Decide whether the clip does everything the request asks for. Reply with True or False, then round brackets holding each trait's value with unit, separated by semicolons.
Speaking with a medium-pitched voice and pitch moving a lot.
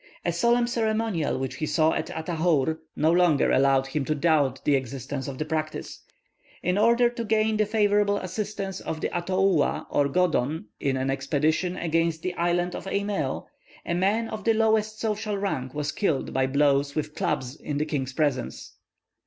True (165 Hz; 6.1 semitones)